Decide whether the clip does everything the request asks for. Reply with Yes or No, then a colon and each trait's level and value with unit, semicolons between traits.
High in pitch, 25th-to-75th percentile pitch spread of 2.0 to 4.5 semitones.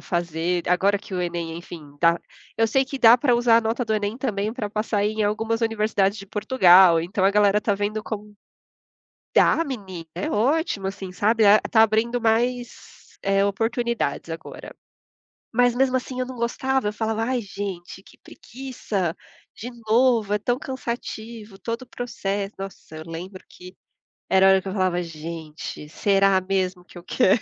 Yes: high, 205 Hz; average, 3.7 semitones